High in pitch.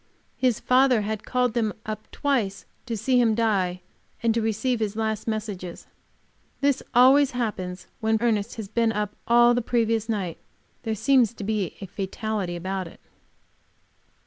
Yes: high, 220 Hz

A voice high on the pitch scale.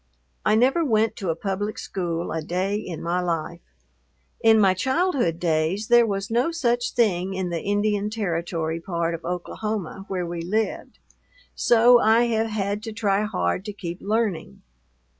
Yes: high, 200 Hz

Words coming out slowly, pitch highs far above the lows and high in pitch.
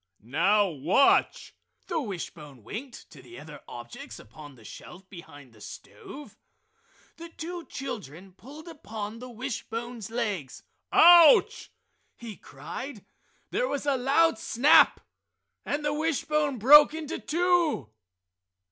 Yes: slow, 115 wpm; wide, 9.0 semitones; high, 240 Hz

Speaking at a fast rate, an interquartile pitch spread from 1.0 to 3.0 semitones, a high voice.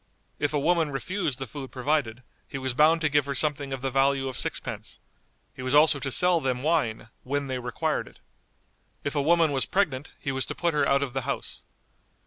No: fast, 215 wpm; narrow, 2.5 semitones; medium, 140 Hz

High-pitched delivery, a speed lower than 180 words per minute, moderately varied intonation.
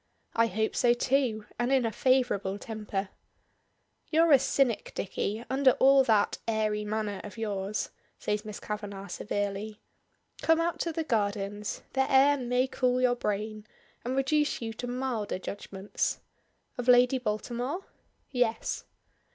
Yes: high, 230 Hz; average, 140 wpm; average, 3.8 semitones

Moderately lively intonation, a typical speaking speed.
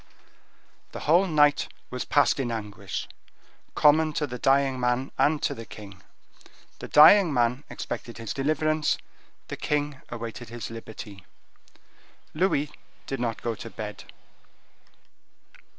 No: average, 4.5 semitones; slow, 125 wpm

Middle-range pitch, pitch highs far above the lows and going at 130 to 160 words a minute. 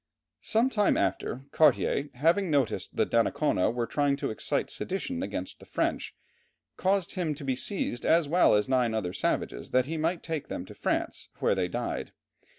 No: medium, 150 Hz; wide, 6.1 semitones; average, 175 wpm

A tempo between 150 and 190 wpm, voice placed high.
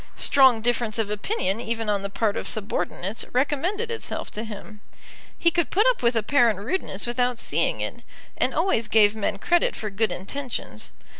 Yes: average, 170 wpm; high, 225 Hz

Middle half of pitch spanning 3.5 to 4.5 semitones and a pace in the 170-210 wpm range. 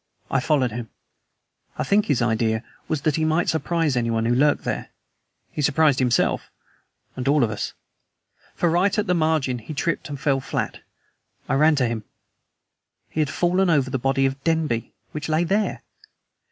Yes: average, 4.2 semitones; average, 175 wpm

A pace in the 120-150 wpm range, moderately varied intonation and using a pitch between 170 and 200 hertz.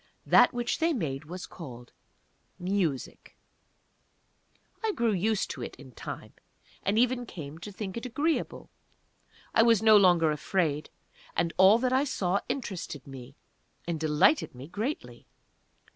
No: average, 140 wpm; wide, 7.5 semitones; medium, 185 Hz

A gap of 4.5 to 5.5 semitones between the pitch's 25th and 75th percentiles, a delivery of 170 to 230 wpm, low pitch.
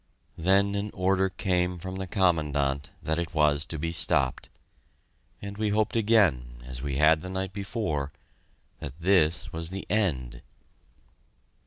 No: average, 4.9 semitones; average, 145 wpm; very low, 85 Hz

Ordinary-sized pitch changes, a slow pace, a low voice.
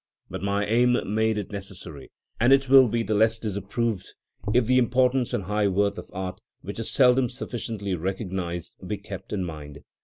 No: average, 3.8 semitones; average, 180 wpm; low, 105 Hz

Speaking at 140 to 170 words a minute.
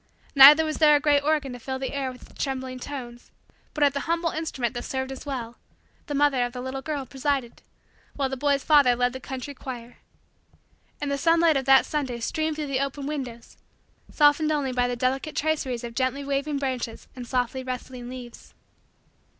No: average, 195 wpm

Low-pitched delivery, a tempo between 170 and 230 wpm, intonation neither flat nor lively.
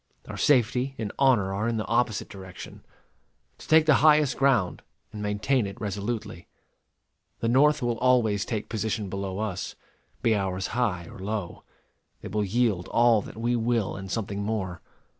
No: low, 110 Hz; average, 160 wpm; average, 3.6 semitones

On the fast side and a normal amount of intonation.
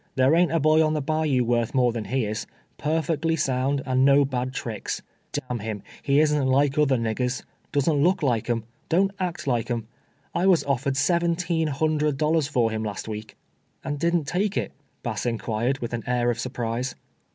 Yes: fast, 210 wpm; average, 4.5 semitones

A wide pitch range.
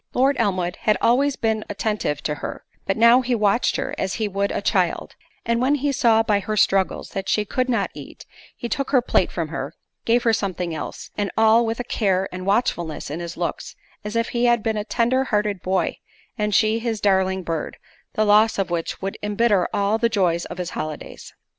No: average, 3.5 semitones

